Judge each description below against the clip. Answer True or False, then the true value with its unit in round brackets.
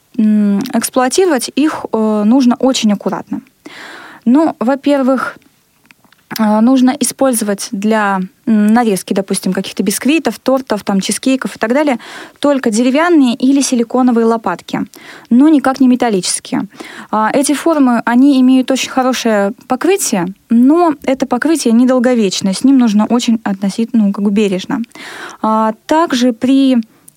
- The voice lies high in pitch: True (245 Hz)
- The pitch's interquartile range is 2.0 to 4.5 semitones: True (3.7 semitones)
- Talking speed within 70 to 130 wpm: True (110 wpm)